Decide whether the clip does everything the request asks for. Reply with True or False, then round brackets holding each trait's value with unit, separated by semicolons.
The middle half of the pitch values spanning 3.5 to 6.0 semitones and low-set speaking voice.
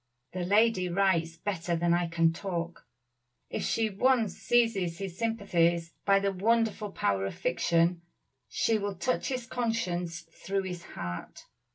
False (4.0 semitones; 185 Hz)